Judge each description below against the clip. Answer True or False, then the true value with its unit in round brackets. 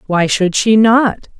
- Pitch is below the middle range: False (205 Hz)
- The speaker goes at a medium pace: True (175 wpm)